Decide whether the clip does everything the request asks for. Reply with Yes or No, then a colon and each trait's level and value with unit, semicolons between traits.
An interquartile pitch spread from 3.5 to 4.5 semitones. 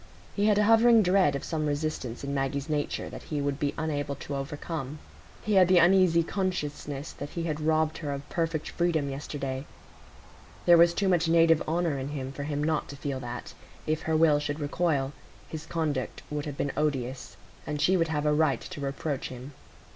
No: average, 2.8 semitones